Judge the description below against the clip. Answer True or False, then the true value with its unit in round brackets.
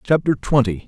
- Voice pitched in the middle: False (125 Hz)